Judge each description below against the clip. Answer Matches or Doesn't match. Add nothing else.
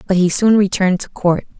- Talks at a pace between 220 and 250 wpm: Matches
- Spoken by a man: Doesn't match